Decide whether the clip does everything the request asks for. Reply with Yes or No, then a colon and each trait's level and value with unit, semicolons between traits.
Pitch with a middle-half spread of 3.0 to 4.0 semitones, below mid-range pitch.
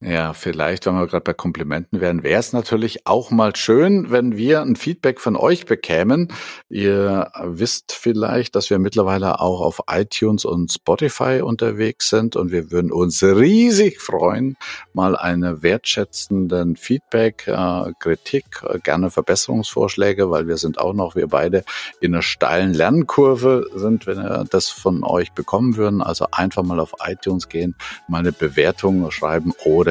No: average, 4.6 semitones; very low, 95 Hz